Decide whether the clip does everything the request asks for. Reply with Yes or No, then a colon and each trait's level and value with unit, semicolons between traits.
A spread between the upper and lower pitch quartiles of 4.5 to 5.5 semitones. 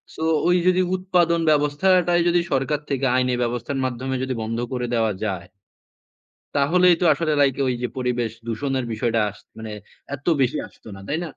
Yes: average, 5.1 semitones